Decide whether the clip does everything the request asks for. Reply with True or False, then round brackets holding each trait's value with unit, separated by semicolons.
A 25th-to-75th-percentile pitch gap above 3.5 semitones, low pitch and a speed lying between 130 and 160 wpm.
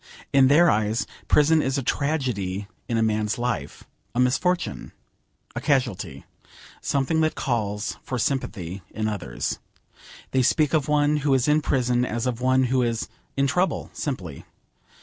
True (4.9 semitones; 125 Hz; 150 wpm)